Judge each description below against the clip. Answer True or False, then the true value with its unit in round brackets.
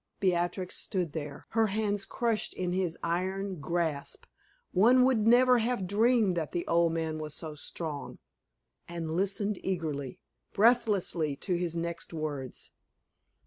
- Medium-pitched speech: True (180 Hz)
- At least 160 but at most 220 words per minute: False (135 wpm)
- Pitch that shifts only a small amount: False (4.2 semitones)